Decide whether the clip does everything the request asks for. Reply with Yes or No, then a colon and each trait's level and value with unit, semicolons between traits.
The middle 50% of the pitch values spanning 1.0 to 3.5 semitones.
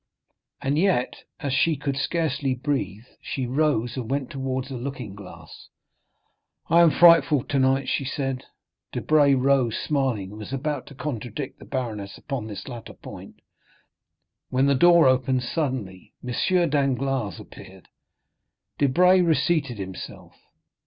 Yes: average, 3.1 semitones